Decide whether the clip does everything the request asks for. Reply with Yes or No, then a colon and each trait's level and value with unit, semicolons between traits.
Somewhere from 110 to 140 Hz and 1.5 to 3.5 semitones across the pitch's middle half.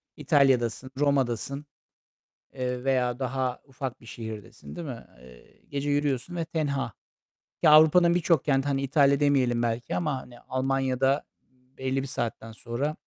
Yes: low, 135 Hz; narrow, 2.6 semitones